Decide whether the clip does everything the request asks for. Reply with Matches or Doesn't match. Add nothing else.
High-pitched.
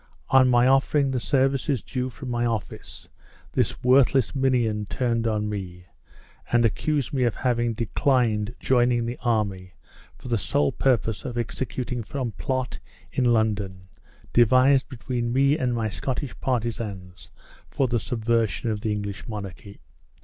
Doesn't match